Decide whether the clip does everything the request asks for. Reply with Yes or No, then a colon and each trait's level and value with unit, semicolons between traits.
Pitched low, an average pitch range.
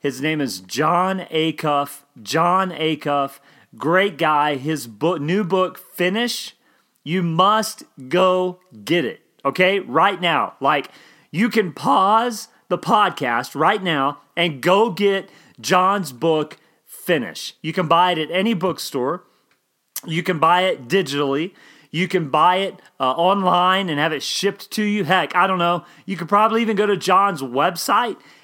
No: medium, 175 Hz; average, 4.1 semitones